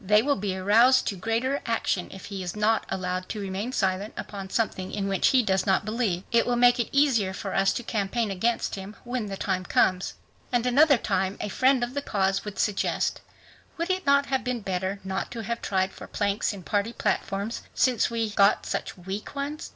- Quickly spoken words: Yes, fast, 210 wpm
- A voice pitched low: No, high, 210 Hz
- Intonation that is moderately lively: Yes, average, 4.0 semitones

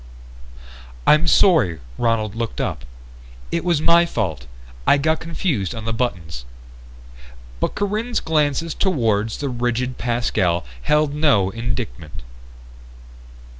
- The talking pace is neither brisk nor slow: No, slow, 110 wpm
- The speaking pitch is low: Yes, low, 120 Hz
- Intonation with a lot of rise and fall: Yes, wide, 7.6 semitones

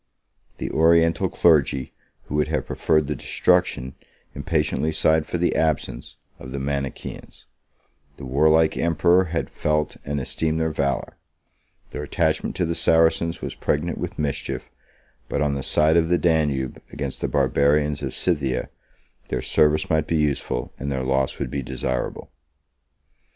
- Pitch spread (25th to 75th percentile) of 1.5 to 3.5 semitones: Yes, narrow, 2.6 semitones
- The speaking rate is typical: Yes, average, 150 wpm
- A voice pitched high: No, very low, 75 Hz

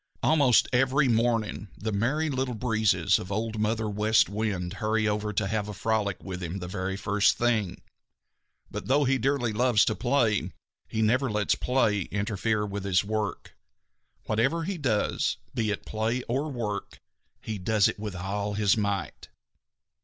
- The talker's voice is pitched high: No, low, 110 Hz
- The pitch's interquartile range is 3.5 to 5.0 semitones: No, average, 3.0 semitones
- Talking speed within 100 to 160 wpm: Yes, average, 155 wpm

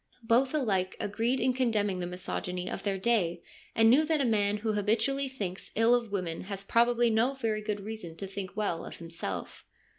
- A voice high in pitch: Yes, high, 215 Hz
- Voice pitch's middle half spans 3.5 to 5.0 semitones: Yes, average, 4.0 semitones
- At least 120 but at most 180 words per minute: No, average, 190 wpm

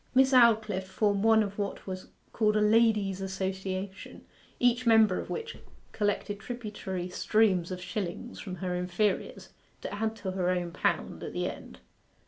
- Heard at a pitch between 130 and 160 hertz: No, high, 205 Hz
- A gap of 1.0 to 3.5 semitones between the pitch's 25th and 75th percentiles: Yes, average, 2.9 semitones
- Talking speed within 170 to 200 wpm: No, average, 155 wpm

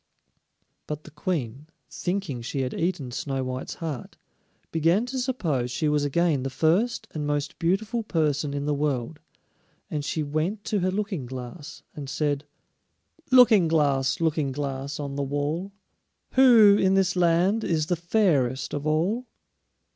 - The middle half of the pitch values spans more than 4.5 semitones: Yes, average, 4.9 semitones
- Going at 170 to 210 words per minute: No, average, 150 wpm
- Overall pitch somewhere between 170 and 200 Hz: No, medium, 155 Hz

